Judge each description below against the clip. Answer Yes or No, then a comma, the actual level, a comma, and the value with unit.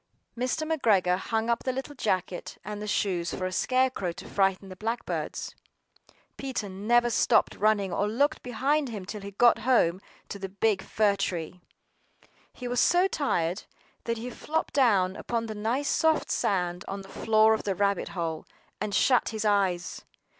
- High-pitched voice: Yes, high, 210 Hz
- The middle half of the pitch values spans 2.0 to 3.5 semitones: No, average, 4.1 semitones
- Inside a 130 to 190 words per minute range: Yes, average, 175 wpm